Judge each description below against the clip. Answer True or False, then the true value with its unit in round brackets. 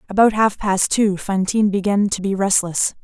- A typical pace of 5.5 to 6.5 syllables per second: False (5.0 syllables/s)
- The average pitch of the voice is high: True (200 Hz)